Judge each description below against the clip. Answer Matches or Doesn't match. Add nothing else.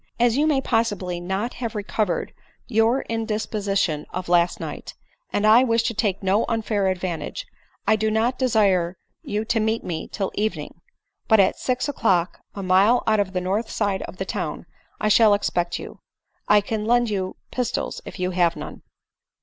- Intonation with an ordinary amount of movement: Matches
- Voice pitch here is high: Matches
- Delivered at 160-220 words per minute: Matches